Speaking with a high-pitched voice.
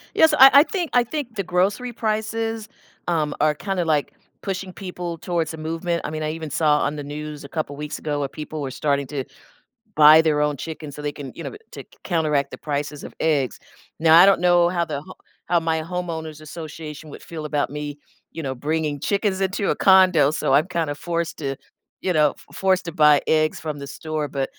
No: medium, 160 Hz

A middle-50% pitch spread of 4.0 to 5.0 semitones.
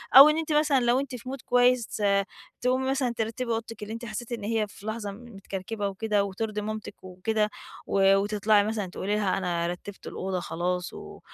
No: average, 3.5 semitones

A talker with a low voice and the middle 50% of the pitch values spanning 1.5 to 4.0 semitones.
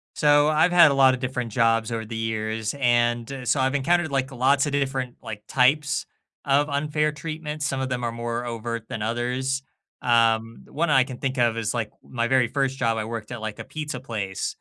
Yes: low, 125 Hz; average, 3.3 semitones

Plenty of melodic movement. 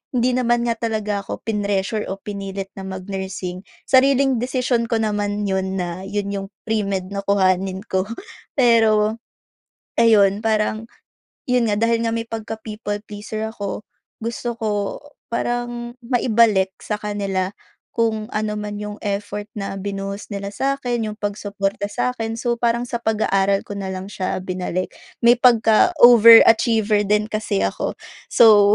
No: average, 2.7 semitones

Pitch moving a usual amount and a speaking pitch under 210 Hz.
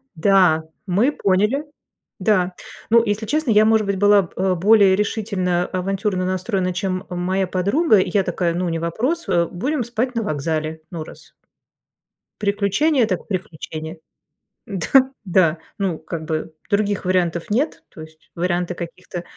Yes: average, 3.4 semitones; medium, 185 Hz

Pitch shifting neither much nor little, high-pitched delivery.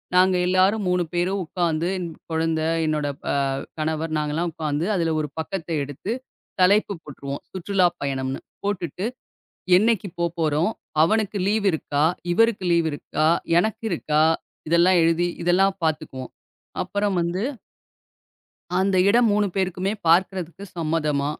No: average, 3.6 semitones; medium, 175 Hz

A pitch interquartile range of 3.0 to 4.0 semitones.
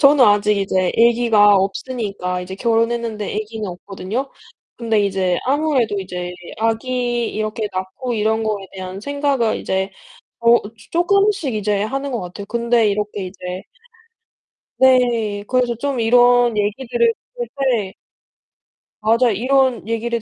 Yes: average, 3.5 semitones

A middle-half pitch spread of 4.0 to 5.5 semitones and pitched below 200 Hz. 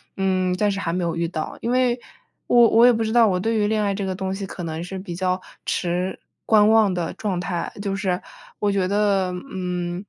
No: narrow, 2.6 semitones; high, 190 Hz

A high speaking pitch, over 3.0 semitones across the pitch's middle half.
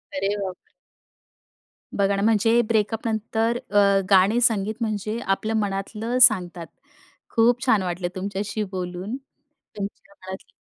No: high, 205 Hz; narrow, 2.6 semitones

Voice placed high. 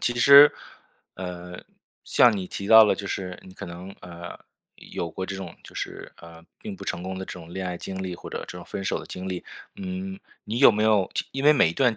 No: very low, 95 Hz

